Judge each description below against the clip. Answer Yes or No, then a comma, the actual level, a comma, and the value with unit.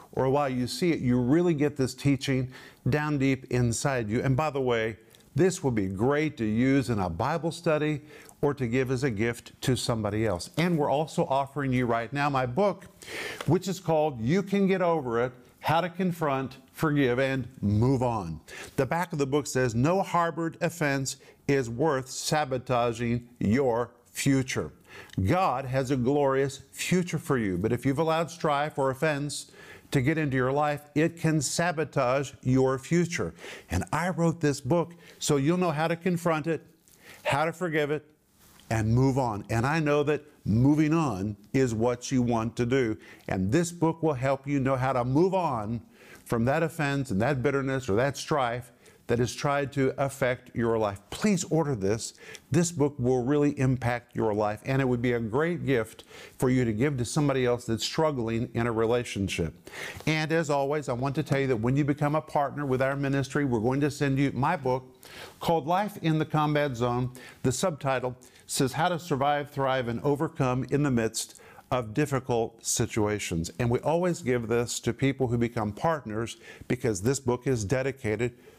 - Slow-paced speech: No, average, 190 wpm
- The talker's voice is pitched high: No, low, 135 Hz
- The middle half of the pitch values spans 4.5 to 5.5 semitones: No, average, 3.8 semitones